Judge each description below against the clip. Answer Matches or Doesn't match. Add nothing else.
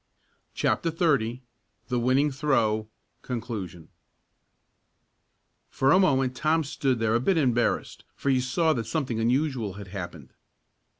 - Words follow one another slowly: Matches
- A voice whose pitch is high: Doesn't match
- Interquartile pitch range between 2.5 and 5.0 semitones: Matches